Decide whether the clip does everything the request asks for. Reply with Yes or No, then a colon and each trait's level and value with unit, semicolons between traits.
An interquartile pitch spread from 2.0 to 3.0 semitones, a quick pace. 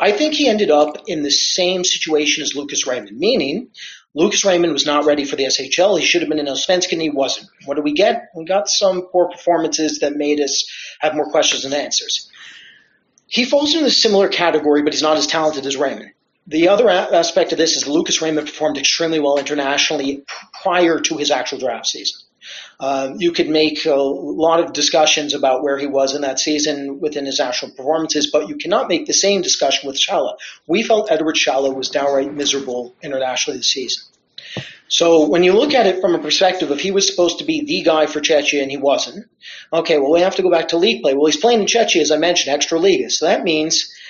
No: average, 3.8 semitones; fast, 220 wpm